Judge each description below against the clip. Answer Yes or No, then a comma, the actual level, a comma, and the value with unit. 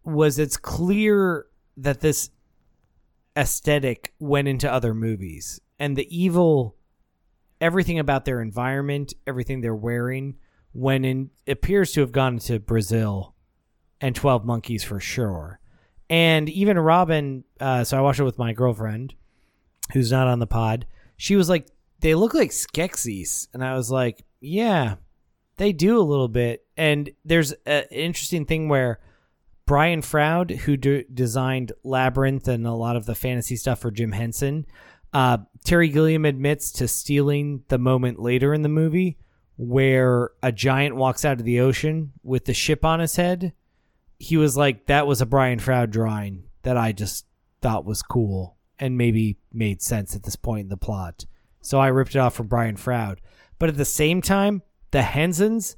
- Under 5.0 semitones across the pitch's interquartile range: Yes, average, 4.5 semitones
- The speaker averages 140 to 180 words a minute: Yes, average, 165 wpm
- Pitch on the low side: Yes, low, 130 Hz